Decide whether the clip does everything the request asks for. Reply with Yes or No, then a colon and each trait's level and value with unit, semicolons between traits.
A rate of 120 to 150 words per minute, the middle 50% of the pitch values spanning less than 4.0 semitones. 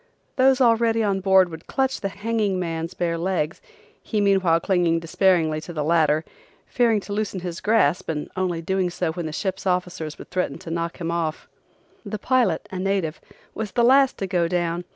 No: average, 190 wpm; average, 3.4 semitones